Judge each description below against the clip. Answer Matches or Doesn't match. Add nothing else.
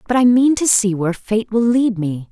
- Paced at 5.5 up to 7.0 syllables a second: Doesn't match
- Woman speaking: Matches